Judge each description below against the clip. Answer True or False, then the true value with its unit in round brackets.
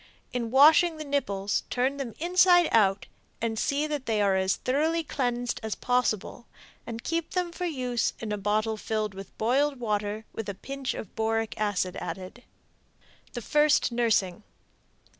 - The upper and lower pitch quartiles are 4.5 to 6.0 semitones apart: True (5.1 semitones)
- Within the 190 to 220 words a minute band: False (160 wpm)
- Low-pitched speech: False (235 Hz)